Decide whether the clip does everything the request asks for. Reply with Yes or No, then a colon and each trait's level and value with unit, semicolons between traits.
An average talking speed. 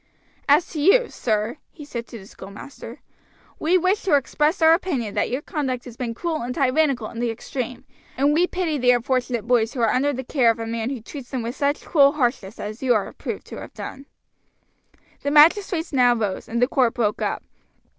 No: fast, 210 wpm